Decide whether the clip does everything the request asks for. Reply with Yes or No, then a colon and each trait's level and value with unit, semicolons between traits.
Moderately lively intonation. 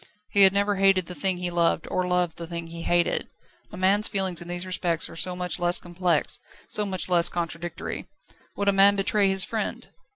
No: narrow, 2.1 semitones